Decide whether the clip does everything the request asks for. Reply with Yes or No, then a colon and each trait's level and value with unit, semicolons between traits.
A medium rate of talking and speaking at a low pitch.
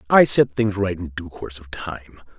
No: fast, 225 wpm; very low, 95 Hz